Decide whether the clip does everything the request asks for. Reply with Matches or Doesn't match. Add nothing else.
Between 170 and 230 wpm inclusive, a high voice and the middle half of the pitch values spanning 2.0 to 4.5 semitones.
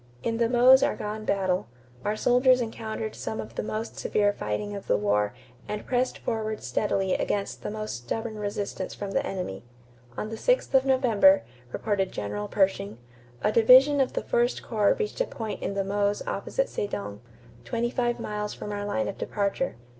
Matches